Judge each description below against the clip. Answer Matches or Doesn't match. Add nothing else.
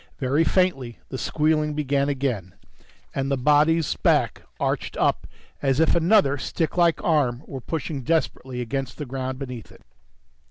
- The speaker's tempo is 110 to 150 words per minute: Matches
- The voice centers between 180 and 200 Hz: Doesn't match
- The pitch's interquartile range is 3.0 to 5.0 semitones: Matches